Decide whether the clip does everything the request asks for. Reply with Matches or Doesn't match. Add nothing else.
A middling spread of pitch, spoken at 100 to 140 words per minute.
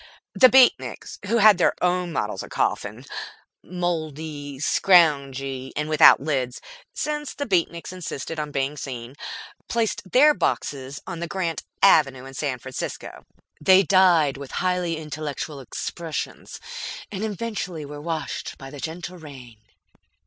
Matches